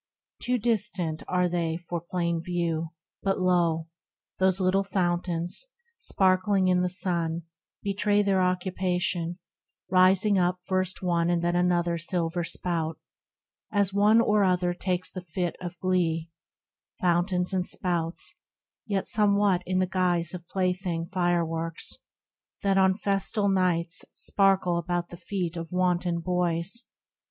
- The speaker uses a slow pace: Yes, slow, 130 wpm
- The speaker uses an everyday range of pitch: No, narrow, 1.8 semitones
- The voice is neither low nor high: Yes, medium, 180 Hz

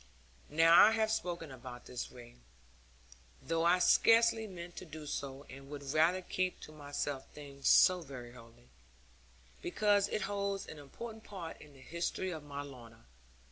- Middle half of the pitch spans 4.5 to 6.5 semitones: Yes, average, 5.2 semitones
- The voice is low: No, medium, 155 Hz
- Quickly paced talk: No, average, 160 wpm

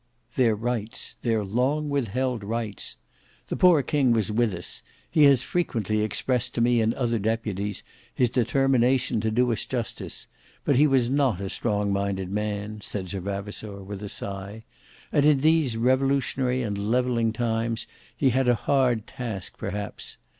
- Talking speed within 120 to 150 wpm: No, average, 160 wpm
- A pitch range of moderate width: Yes, average, 3.8 semitones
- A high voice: No, low, 115 Hz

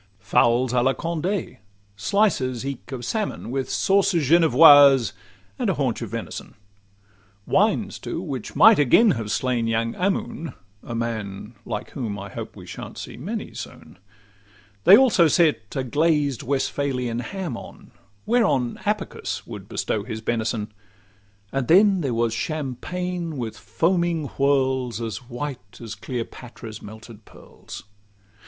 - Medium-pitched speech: No, low, 130 Hz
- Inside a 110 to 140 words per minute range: Yes, slow, 135 wpm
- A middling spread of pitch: No, wide, 6.4 semitones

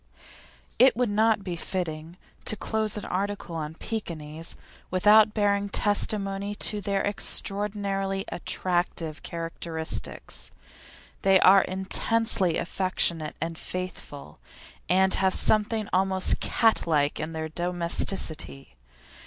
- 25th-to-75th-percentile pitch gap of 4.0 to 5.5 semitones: No, average, 3.5 semitones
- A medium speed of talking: No, slow, 105 wpm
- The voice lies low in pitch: No, high, 190 Hz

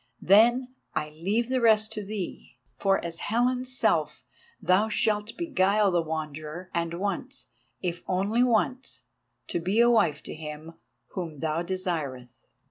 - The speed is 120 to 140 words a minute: Yes, slow, 135 wpm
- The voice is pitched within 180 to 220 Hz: Yes, high, 190 Hz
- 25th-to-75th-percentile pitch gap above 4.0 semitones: Yes, average, 5.2 semitones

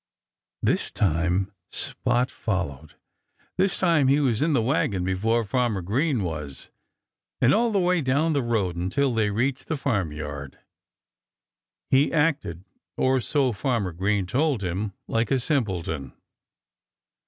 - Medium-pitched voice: No, low, 115 Hz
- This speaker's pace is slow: Yes, slow, 130 wpm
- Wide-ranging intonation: Yes, wide, 7.2 semitones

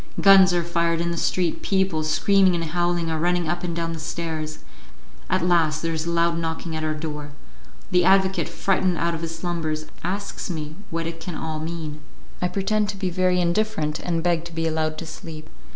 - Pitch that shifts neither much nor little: No, narrow, 2.0 semitones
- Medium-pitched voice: Yes, medium, 170 Hz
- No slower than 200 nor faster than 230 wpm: Yes, fast, 205 wpm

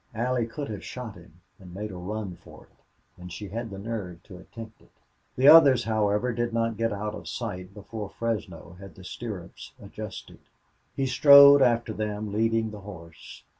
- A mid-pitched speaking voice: No, low, 110 Hz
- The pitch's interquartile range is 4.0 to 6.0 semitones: No, average, 3.2 semitones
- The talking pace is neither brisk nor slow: Yes, average, 180 wpm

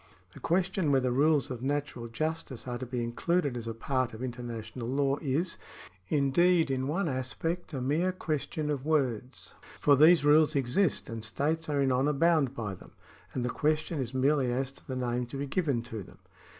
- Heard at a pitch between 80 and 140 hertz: Yes, low, 135 Hz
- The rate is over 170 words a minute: Yes, average, 195 wpm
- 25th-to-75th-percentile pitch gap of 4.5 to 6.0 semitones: No, average, 3.8 semitones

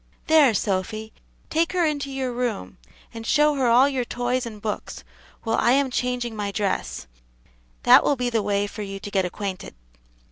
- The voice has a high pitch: Yes, high, 235 Hz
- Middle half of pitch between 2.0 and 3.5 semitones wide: No, average, 4.4 semitones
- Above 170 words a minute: Yes, average, 180 wpm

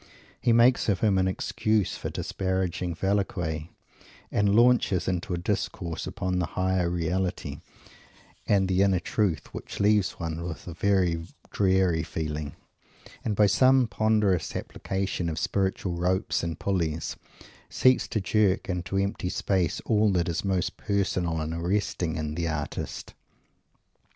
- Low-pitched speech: Yes, very low, 95 Hz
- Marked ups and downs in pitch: No, average, 2.9 semitones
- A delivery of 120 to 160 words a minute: Yes, average, 140 wpm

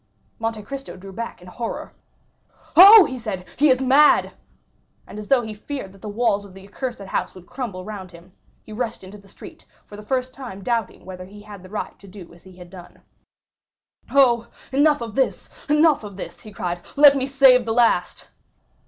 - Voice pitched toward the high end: Yes, high, 215 Hz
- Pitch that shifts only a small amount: No, average, 5.2 semitones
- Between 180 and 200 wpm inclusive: Yes, average, 195 wpm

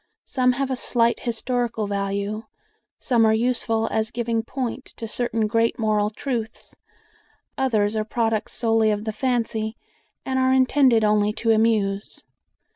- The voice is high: Yes, high, 225 Hz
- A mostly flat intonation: Yes, narrow, 2.2 semitones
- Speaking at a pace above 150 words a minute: No, average, 140 wpm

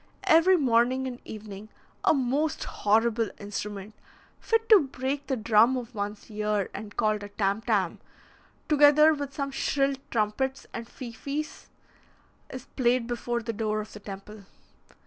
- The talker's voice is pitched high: Yes, high, 235 Hz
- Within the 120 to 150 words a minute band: Yes, average, 145 wpm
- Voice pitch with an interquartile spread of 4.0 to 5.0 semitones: Yes, average, 4.4 semitones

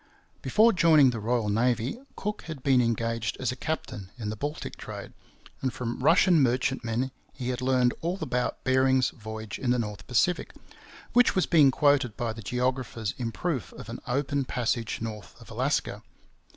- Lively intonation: No, average, 3.5 semitones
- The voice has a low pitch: Yes, low, 125 Hz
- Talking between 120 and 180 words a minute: Yes, average, 170 wpm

